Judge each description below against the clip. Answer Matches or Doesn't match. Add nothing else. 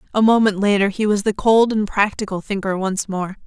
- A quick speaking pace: Matches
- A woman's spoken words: Matches